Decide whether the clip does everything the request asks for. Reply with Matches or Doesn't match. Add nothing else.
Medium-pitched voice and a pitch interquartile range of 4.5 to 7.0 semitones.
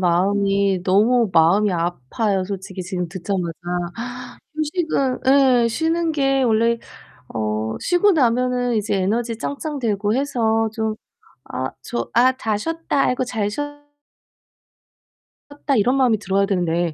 Doesn't match